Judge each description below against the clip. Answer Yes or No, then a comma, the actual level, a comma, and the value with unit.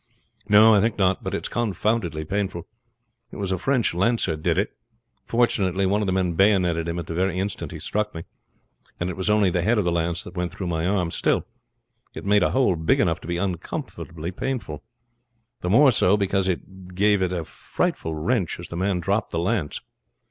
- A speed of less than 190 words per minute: No, fast, 205 wpm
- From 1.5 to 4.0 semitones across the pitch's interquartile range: Yes, average, 3.1 semitones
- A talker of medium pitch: No, very low, 95 Hz